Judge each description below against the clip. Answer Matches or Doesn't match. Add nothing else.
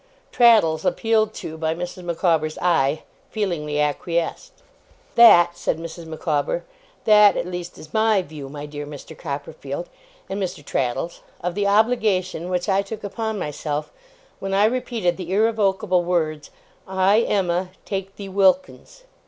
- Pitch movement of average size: Matches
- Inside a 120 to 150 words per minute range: Matches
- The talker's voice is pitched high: Doesn't match